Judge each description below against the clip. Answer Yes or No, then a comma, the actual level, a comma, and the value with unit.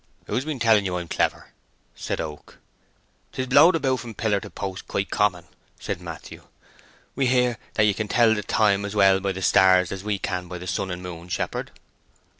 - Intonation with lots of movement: No, average, 3.9 semitones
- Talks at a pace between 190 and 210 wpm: Yes, average, 200 wpm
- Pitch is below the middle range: Yes, low, 100 Hz